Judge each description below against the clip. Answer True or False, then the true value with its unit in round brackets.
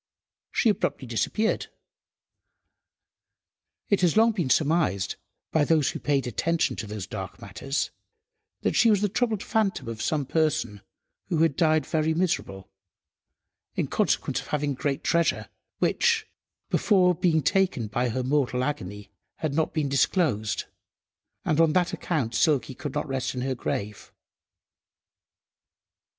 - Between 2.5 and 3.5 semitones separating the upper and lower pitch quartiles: False (5.4 semitones)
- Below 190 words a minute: True (135 wpm)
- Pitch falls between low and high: True (150 Hz)